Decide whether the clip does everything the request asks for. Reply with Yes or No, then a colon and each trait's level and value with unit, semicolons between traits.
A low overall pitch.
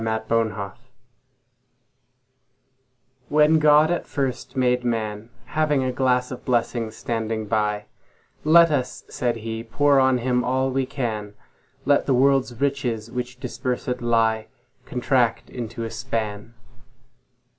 Yes: low, 125 Hz